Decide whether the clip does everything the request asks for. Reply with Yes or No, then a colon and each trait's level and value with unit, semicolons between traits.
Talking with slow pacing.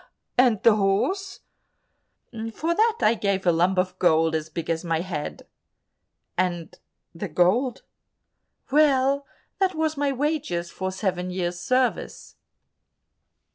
Yes: slow, 125 wpm